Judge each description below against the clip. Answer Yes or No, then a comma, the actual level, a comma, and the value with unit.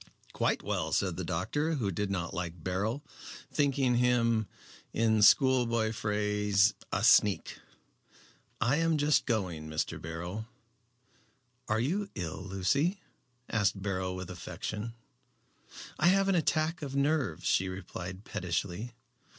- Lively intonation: Yes, wide, 6.9 semitones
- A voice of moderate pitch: No, low, 110 Hz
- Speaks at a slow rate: Yes, slow, 125 wpm